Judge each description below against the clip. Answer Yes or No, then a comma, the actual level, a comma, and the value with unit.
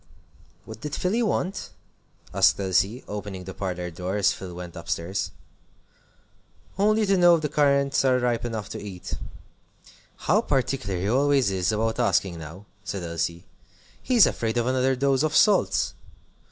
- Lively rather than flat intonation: Yes, wide, 7.0 semitones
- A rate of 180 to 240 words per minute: No, average, 155 wpm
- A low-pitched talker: Yes, low, 110 Hz